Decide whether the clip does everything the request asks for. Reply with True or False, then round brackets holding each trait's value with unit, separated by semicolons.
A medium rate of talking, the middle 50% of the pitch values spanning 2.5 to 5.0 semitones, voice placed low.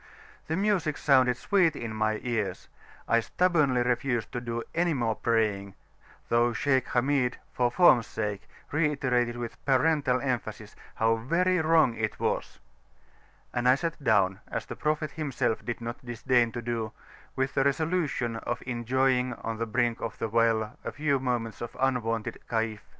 True (155 wpm; 3.6 semitones; 125 Hz)